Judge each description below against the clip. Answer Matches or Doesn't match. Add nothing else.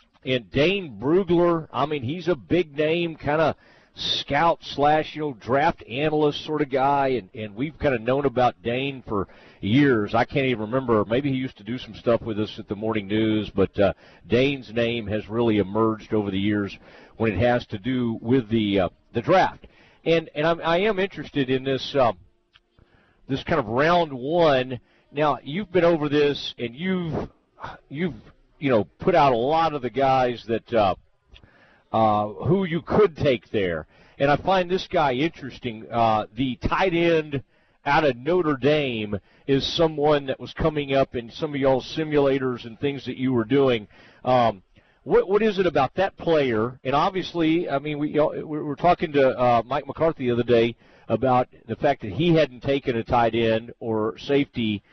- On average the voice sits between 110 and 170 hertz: Matches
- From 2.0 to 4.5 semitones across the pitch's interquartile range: Doesn't match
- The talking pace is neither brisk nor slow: Matches